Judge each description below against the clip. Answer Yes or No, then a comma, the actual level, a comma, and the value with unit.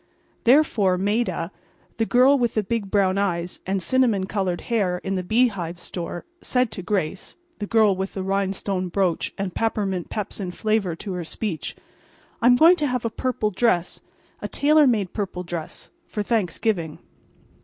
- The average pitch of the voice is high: Yes, high, 200 Hz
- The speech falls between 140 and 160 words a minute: Yes, average, 145 wpm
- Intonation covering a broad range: No, average, 4.2 semitones